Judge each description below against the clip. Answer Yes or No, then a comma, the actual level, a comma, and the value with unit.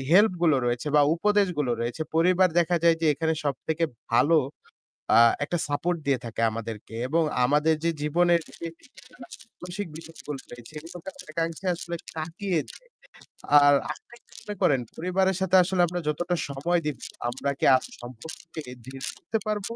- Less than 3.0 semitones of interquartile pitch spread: No, average, 3.6 semitones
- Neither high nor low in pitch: Yes, medium, 165 Hz